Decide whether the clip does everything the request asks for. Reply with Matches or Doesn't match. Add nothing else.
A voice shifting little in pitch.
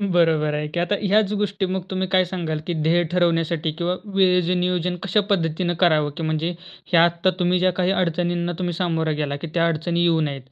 Matches